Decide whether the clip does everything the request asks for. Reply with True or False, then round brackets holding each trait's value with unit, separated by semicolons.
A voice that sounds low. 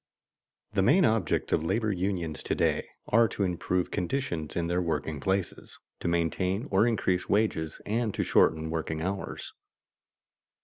True (90 Hz)